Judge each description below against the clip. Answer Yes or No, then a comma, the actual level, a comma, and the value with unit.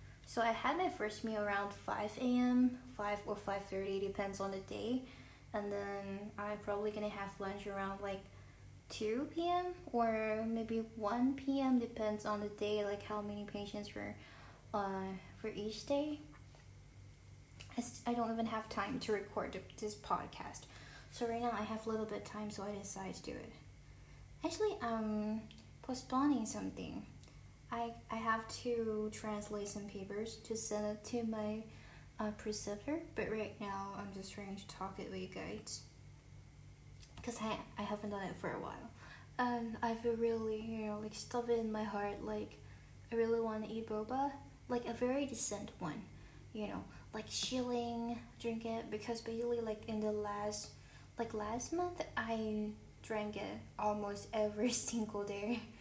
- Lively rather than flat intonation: No, narrow, 2.4 semitones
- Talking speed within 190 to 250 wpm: No, average, 165 wpm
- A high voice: Yes, high, 215 Hz